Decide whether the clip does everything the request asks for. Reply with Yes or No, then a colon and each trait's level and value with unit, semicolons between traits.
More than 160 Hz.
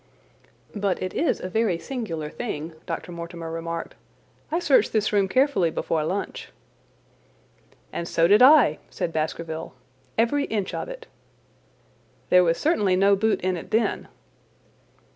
Yes: medium, 185 Hz